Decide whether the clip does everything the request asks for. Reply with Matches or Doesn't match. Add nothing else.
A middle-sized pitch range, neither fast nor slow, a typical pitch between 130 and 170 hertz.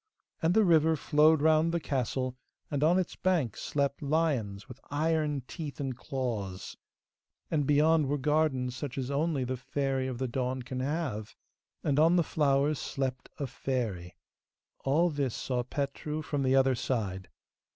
Matches